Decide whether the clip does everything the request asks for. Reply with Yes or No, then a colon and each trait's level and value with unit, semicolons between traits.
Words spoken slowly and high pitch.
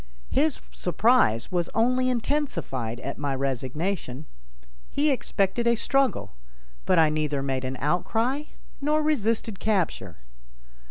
Yes: slow, 115 wpm; high, 195 Hz